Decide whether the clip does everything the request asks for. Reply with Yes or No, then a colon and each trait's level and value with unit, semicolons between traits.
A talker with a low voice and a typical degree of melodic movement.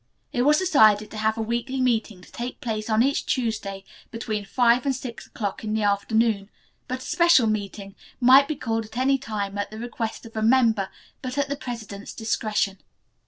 No: high, 225 Hz; average, 3.0 semitones